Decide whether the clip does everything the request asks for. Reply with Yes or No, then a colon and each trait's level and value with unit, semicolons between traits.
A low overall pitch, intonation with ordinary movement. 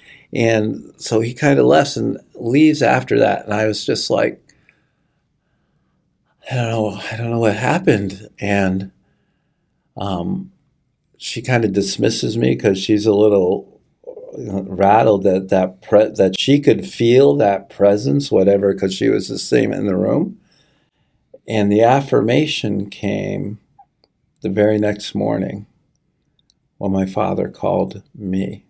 No: low, 110 Hz; wide, 5.8 semitones